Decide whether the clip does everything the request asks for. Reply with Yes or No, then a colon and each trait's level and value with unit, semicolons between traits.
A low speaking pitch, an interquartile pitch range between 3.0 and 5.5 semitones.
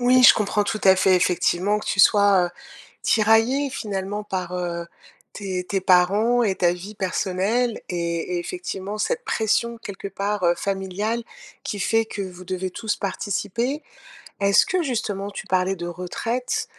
No: high, 200 Hz; average, 3.3 semitones